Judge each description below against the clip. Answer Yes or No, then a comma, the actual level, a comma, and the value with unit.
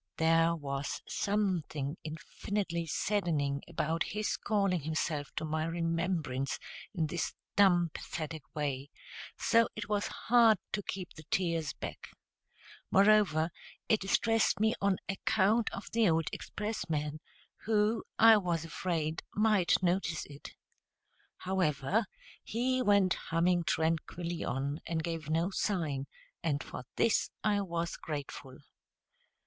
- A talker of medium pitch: Yes, medium, 170 Hz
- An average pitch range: Yes, average, 4.5 semitones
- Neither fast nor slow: No, slow, 120 wpm